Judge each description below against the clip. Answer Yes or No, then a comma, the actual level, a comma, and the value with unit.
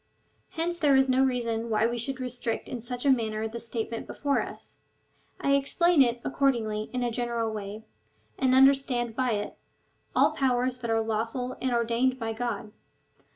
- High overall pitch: Yes, high, 240 Hz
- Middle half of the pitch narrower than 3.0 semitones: Yes, narrow, 2.6 semitones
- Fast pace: No, average, 175 wpm